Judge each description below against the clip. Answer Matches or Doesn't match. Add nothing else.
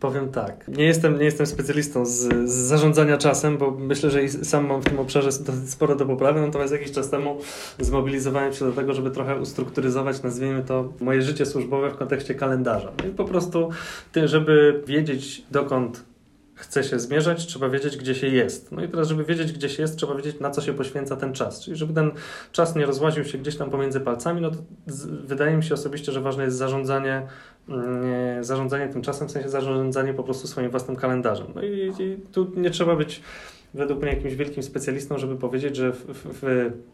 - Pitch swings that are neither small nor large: Doesn't match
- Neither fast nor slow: Doesn't match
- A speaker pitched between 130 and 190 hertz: Matches